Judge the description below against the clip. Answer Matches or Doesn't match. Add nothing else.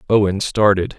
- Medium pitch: Doesn't match